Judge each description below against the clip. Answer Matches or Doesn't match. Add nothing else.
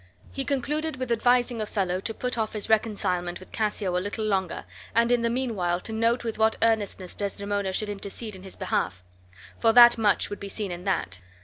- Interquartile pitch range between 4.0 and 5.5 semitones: Doesn't match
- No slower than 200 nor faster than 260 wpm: Matches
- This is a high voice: Matches